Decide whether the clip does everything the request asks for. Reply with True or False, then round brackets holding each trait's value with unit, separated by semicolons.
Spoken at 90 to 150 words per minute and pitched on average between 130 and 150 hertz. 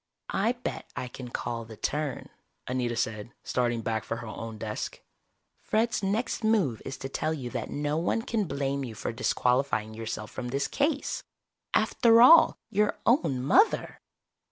False (160 wpm; 135 Hz)